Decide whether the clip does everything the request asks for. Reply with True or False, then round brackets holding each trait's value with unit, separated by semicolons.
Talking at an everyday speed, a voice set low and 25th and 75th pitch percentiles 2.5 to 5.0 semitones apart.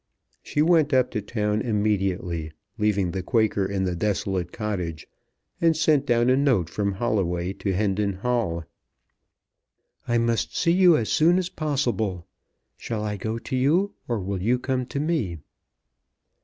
False (155 wpm; 105 Hz; 5.4 semitones)